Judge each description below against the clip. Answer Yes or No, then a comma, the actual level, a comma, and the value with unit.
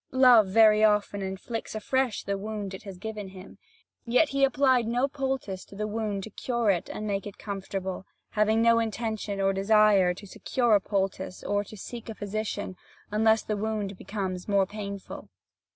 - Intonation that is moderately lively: No, narrow, 2.2 semitones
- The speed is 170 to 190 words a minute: Yes, average, 175 wpm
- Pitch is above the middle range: Yes, high, 210 Hz